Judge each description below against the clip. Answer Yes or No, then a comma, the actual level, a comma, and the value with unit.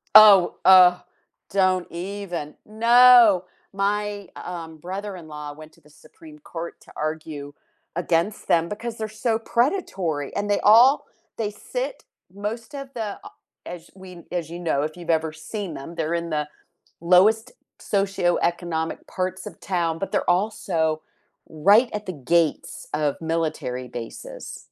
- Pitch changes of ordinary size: Yes, average, 4.4 semitones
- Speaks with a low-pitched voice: No, medium, 180 Hz